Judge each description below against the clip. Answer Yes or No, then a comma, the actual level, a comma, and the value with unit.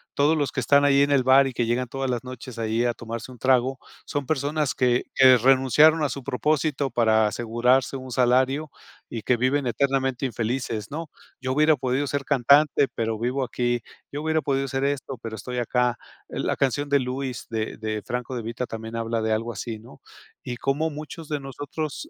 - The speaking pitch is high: No, low, 130 Hz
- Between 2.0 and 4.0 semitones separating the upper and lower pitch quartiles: Yes, average, 3.0 semitones